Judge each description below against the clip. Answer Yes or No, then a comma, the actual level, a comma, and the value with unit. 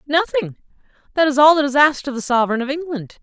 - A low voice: No, very high, 275 Hz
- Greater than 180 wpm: Yes, fast, 205 wpm